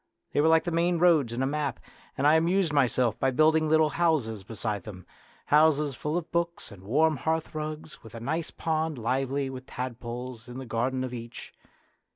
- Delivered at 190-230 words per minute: Yes, average, 195 wpm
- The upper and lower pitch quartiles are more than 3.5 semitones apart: Yes, average, 4.6 semitones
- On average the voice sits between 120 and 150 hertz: Yes, medium, 140 Hz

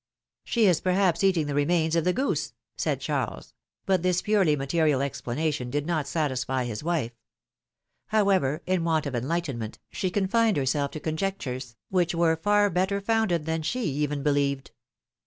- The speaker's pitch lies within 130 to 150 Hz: No, medium, 160 Hz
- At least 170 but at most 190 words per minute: No, average, 155 wpm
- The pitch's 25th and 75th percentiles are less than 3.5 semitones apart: No, average, 4.8 semitones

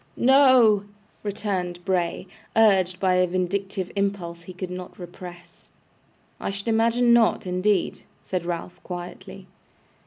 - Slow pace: Yes, slow, 120 wpm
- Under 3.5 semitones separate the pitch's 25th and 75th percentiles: Yes, narrow, 2.6 semitones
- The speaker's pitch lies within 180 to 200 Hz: Yes, high, 190 Hz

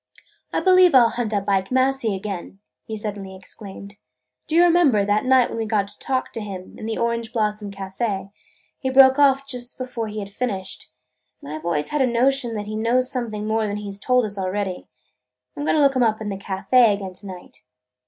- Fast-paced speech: Yes, fast, 220 wpm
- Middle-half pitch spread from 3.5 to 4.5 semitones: Yes, average, 4.2 semitones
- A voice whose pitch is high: Yes, high, 215 Hz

